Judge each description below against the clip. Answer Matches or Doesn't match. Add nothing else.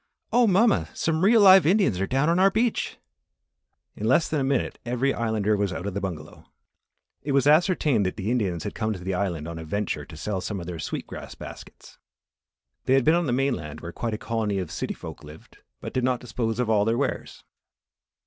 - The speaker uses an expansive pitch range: Matches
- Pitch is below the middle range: Matches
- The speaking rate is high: Matches